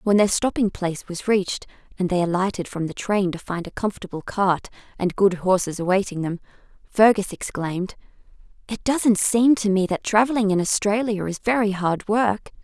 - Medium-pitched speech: No, high, 200 Hz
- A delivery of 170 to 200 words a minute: Yes, average, 175 wpm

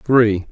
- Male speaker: Yes, male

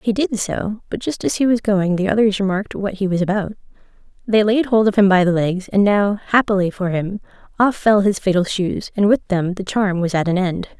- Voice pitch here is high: Yes, high, 200 Hz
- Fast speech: Yes, fast, 235 wpm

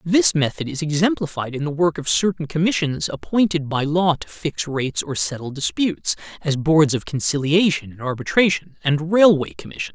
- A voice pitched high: No, medium, 155 Hz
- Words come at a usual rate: Yes, average, 170 wpm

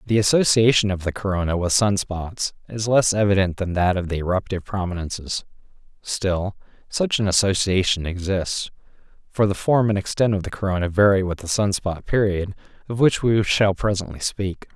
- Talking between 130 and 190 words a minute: Yes, average, 170 wpm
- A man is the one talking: Yes, male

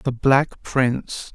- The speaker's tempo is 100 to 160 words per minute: Yes, slow, 135 wpm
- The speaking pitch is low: Yes, low, 130 Hz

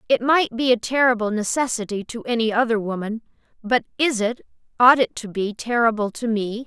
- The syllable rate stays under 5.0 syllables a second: No, 5.4 syllables/s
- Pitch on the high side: Yes, high, 230 Hz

